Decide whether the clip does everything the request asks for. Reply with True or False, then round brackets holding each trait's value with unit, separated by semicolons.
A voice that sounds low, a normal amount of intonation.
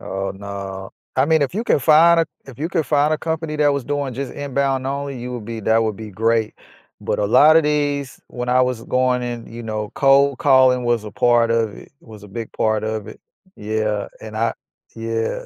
True (125 Hz; 4.3 semitones)